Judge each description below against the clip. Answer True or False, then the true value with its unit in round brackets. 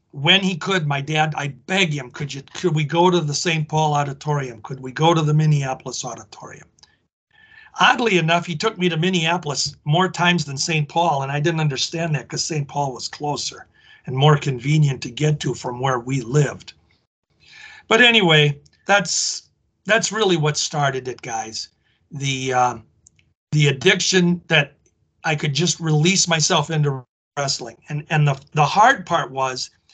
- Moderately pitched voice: True (150 Hz)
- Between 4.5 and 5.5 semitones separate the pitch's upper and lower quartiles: False (3.7 semitones)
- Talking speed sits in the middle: True (170 wpm)